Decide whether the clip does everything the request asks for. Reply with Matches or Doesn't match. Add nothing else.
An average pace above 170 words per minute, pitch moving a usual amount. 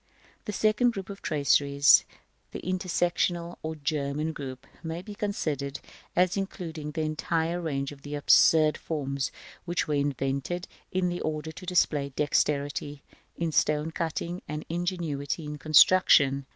Doesn't match